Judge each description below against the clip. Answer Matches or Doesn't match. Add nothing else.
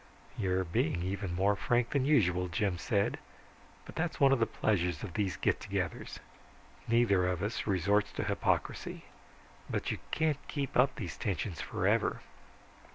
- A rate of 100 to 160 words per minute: Matches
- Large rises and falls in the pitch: Doesn't match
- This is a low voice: Matches